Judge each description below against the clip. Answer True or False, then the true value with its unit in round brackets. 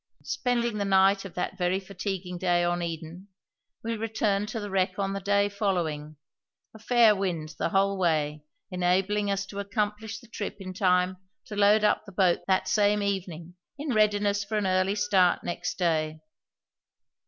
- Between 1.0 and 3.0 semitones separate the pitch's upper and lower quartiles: True (2.4 semitones)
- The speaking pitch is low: False (195 Hz)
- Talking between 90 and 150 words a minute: False (170 wpm)